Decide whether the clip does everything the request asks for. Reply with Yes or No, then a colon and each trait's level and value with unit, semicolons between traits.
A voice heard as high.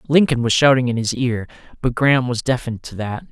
No: low, 125 Hz